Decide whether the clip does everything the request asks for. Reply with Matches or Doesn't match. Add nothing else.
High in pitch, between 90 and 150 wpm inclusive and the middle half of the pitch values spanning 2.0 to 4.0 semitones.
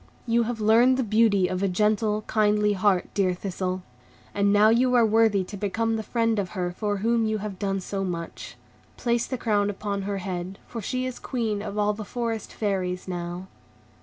Doesn't match